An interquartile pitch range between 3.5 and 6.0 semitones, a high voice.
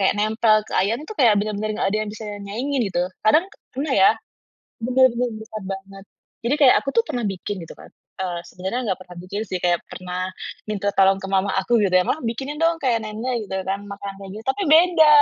Yes: average, 4.3 semitones; high, 215 Hz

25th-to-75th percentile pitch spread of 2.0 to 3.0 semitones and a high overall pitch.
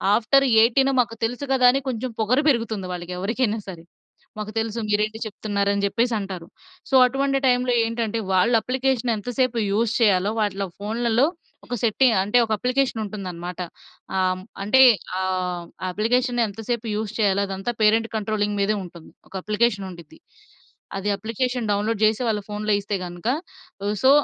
No: average, 3.4 semitones; high, 220 Hz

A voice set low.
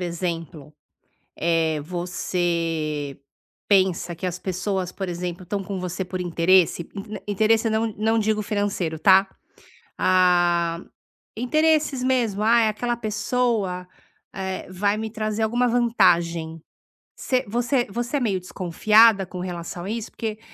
No: high, 190 Hz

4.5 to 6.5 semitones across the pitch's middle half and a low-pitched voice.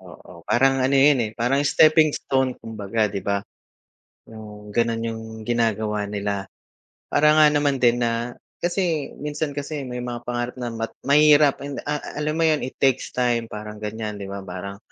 Yes: average, 5.0 semitones; low, 120 Hz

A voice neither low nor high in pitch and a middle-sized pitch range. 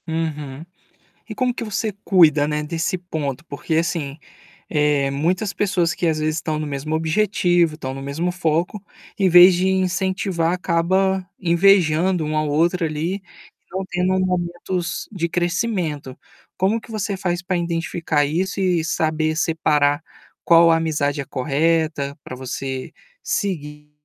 Yes: medium, 165 Hz; average, 3.4 semitones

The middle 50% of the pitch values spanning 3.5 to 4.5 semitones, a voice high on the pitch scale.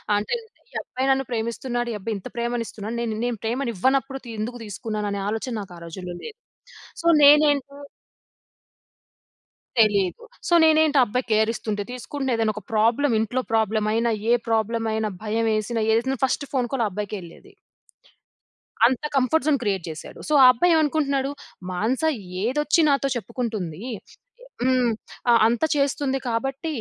Yes: average, 4.0 semitones; high, 235 Hz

